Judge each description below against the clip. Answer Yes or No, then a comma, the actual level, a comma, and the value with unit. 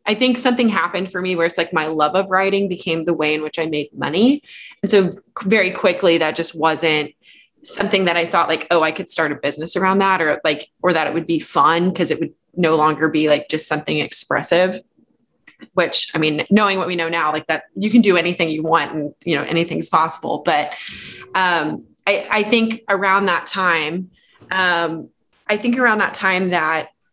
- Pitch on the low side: No, medium, 170 Hz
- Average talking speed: No, fast, 210 wpm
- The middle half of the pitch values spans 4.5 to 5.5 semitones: No, average, 3.6 semitones